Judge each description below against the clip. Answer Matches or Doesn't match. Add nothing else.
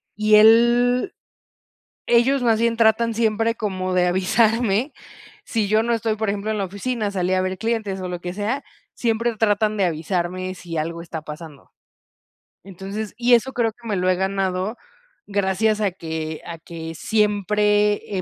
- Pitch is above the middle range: Matches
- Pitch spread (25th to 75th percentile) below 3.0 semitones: Doesn't match